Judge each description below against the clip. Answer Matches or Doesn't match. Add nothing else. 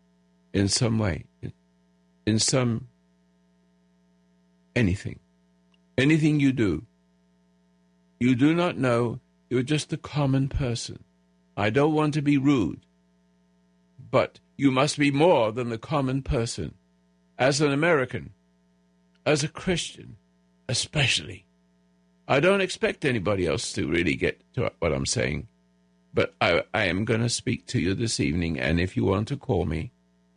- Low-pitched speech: Matches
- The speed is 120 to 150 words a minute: Matches